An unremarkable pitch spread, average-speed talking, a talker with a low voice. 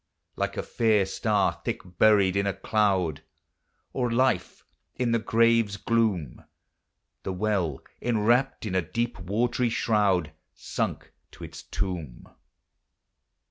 No: average, 3.7 semitones; slow, 120 wpm; low, 105 Hz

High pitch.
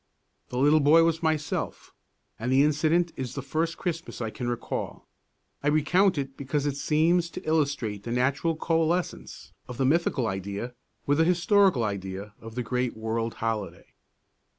No: medium, 140 Hz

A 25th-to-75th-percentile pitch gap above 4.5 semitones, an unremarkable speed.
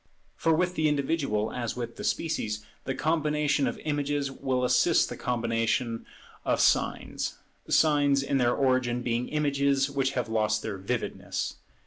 No: average, 3.6 semitones; average, 145 wpm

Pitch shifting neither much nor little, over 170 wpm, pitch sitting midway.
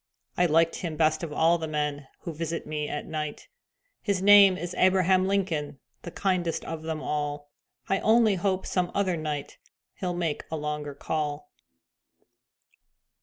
No: average, 3.6 semitones; average, 155 wpm; medium, 165 Hz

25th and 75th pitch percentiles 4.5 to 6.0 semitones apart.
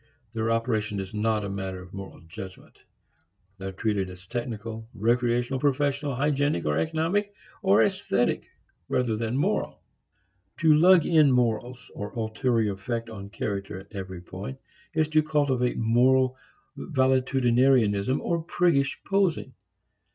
Yes: wide, 5.4 semitones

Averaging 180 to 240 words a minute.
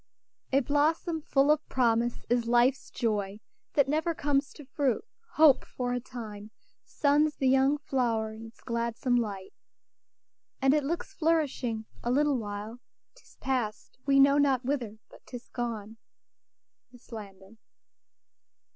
No: average, 140 wpm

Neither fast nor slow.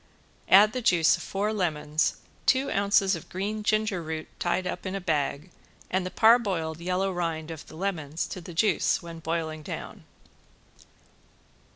Yes: average, 160 wpm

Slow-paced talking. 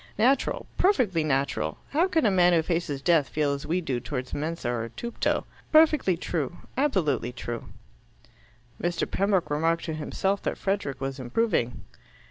No: average, 150 wpm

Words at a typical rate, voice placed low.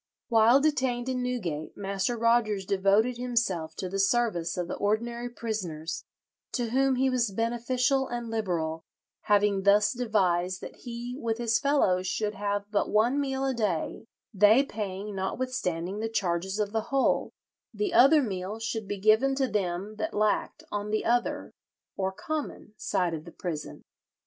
No: average, 160 wpm; high, 215 Hz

